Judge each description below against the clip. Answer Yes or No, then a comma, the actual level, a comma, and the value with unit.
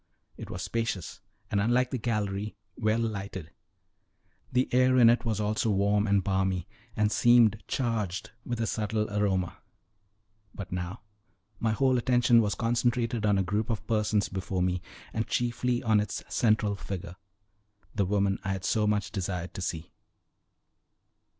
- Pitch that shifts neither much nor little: Yes, average, 3.0 semitones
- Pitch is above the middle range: No, low, 105 Hz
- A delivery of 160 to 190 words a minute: No, average, 150 wpm